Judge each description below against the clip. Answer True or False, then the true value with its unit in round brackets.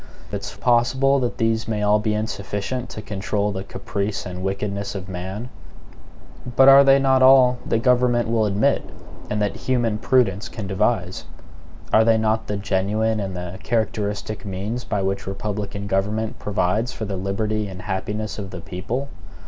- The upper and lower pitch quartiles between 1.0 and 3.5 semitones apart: True (2.9 semitones)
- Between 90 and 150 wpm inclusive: False (165 wpm)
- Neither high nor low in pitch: False (105 Hz)